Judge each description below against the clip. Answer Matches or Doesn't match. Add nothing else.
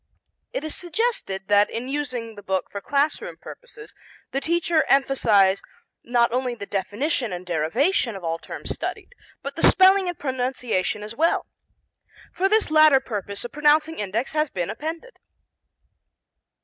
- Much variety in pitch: Matches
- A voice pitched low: Doesn't match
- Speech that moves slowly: Doesn't match